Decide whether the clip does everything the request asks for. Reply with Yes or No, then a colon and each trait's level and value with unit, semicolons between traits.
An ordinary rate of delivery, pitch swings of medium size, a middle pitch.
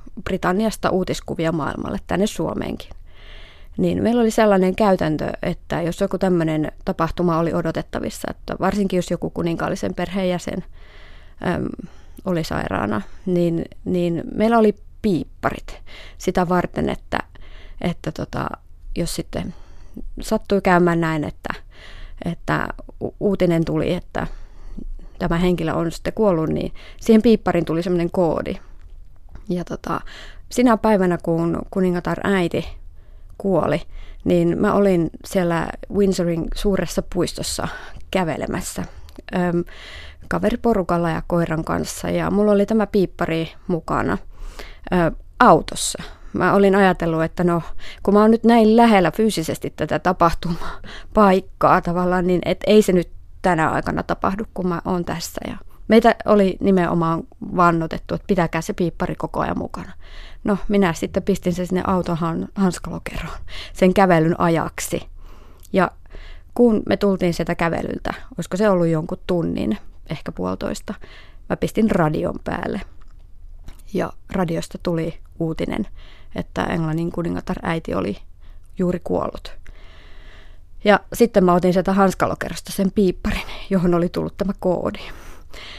Yes: average, 125 wpm; average, 3.7 semitones; medium, 175 Hz